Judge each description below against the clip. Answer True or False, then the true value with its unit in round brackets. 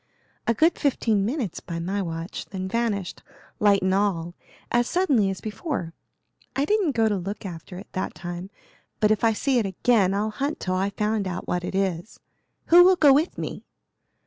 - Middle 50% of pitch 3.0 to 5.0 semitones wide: True (4.5 semitones)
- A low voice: False (205 Hz)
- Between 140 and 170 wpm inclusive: False (190 wpm)